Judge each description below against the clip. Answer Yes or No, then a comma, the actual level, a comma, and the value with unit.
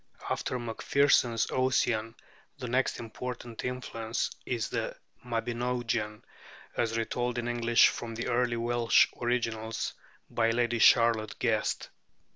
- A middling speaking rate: No, slow, 110 wpm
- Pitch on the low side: Yes, low, 120 Hz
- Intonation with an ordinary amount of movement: No, narrow, 1.2 semitones